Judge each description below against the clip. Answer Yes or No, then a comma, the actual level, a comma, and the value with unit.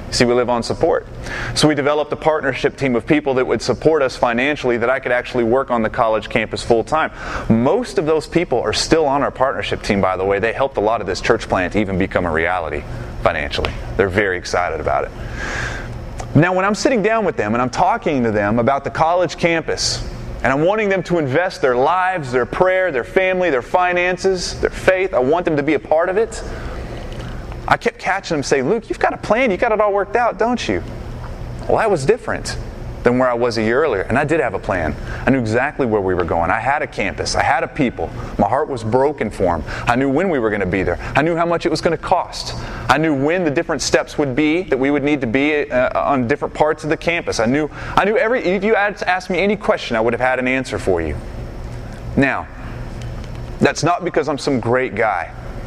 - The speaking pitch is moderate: Yes, medium, 145 Hz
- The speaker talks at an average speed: No, fast, 240 wpm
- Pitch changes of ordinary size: No, wide, 6.5 semitones